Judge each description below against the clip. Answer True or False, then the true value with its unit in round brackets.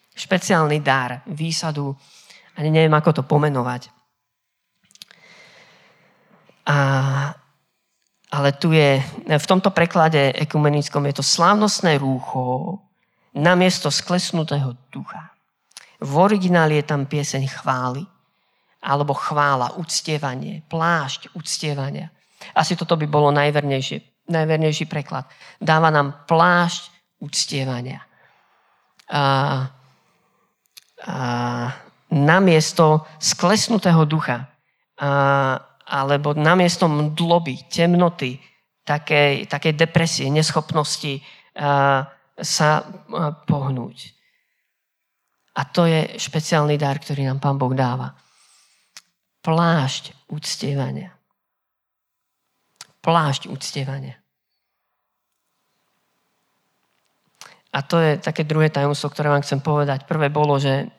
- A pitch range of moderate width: True (3.1 semitones)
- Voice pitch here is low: False (150 Hz)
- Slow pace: True (90 wpm)